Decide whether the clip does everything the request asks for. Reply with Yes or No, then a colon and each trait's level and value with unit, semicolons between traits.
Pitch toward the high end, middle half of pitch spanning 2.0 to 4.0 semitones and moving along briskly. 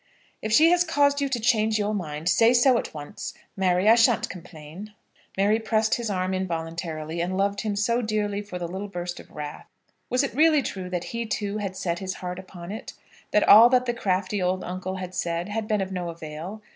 Yes: high, 200 Hz; average, 3.7 semitones; fast, 215 wpm